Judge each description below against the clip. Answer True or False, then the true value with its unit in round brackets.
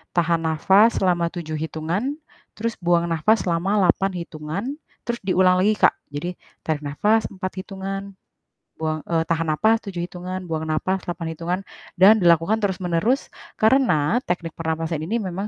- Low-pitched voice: False (175 Hz)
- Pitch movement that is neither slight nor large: True (3.1 semitones)